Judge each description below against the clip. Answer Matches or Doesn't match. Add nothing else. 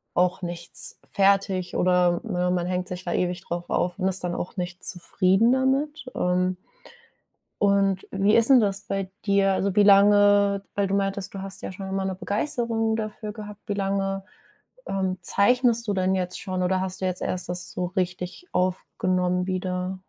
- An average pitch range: Doesn't match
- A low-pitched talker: Doesn't match